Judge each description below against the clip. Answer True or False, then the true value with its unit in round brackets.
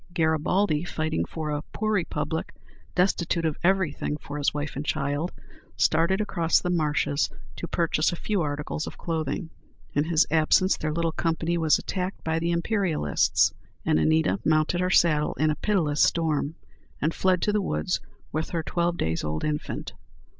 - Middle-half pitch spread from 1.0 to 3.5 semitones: True (2.7 semitones)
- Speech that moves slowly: False (165 wpm)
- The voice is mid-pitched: True (160 Hz)